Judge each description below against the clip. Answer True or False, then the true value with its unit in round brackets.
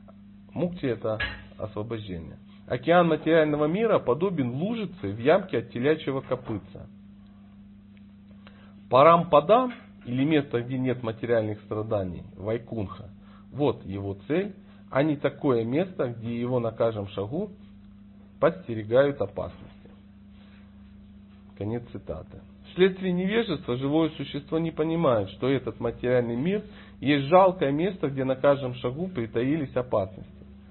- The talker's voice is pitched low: True (115 Hz)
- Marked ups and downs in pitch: True (6.5 semitones)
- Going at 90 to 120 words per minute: True (110 wpm)